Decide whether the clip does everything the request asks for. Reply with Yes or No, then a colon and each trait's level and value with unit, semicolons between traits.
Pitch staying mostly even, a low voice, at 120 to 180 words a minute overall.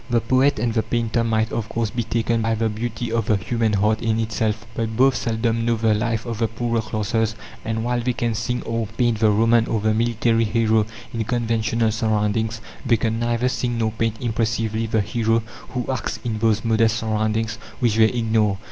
No: narrow, 1.1 semitones; low, 115 Hz; average, 200 wpm